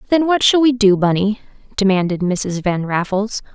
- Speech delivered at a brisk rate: No, average, 170 wpm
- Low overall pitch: No, high, 210 Hz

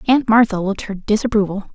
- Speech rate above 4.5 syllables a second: Yes, 6.3 syllables/s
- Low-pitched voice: No, high, 210 Hz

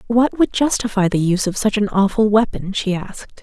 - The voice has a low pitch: No, high, 210 Hz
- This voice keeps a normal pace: No, fast, 210 wpm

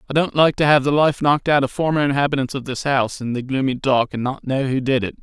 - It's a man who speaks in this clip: Yes, male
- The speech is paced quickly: Yes, fast, 285 wpm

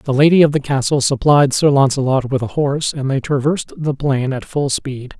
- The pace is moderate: No, fast, 220 wpm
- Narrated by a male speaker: Yes, male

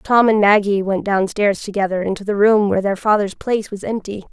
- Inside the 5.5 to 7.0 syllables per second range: Yes, 5.7 syllables/s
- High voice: Yes, high, 205 Hz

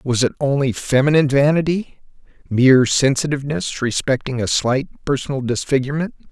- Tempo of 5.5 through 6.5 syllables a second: Yes, 5.6 syllables/s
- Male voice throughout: Yes, male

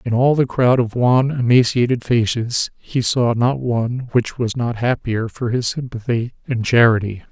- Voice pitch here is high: No, low, 120 Hz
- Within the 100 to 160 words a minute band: No, average, 170 wpm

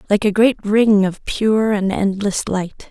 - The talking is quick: No, average, 185 wpm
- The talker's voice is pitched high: Yes, high, 205 Hz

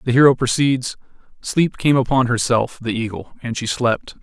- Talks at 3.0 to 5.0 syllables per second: Yes, 4.9 syllables/s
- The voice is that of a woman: No, male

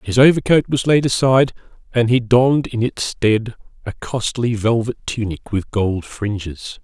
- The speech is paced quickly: No, average, 160 wpm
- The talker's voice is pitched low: Yes, low, 115 Hz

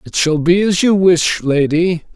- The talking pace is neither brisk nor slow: Yes, average, 195 wpm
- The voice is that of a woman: No, male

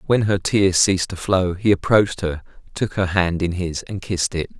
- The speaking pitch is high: No, very low, 95 Hz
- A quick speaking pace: Yes, fast, 220 wpm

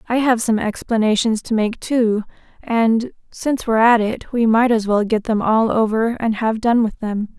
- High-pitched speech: Yes, high, 225 Hz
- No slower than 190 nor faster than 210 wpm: Yes, fast, 205 wpm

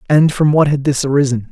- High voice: No, medium, 140 Hz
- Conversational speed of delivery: No, fast, 240 wpm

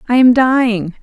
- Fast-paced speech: No, average, 175 wpm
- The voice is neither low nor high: No, high, 240 Hz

